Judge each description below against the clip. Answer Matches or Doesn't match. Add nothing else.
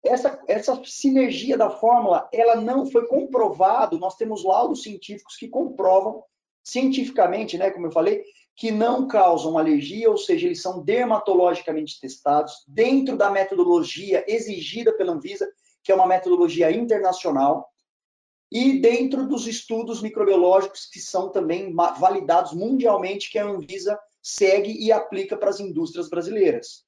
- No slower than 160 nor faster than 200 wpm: Doesn't match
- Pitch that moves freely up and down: Matches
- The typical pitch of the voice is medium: Doesn't match